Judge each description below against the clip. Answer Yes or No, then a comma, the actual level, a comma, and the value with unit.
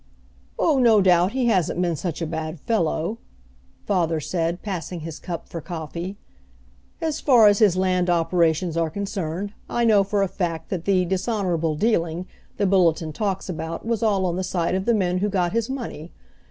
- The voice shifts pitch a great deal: No, average, 3.5 semitones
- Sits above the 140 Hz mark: Yes, medium, 185 Hz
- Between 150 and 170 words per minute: No, average, 180 wpm